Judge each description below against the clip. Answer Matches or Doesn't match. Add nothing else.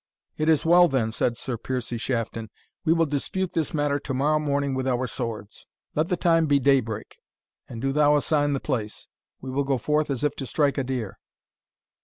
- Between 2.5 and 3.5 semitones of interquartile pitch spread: Matches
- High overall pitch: Doesn't match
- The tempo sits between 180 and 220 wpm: Matches